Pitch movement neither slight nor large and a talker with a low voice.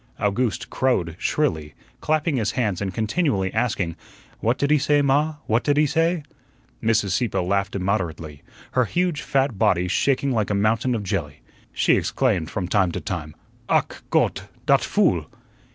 No: wide, 6.5 semitones; low, 110 Hz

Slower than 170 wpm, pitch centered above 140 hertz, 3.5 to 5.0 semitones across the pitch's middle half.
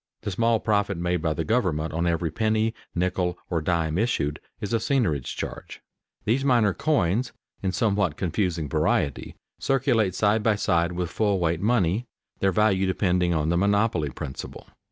No: average, 160 wpm; very low, 95 Hz; average, 4.6 semitones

